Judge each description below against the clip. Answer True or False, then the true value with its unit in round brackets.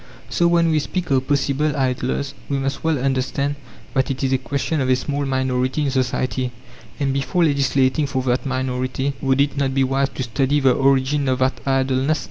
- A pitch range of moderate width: False (1.4 semitones)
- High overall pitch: False (135 Hz)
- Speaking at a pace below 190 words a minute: False (195 wpm)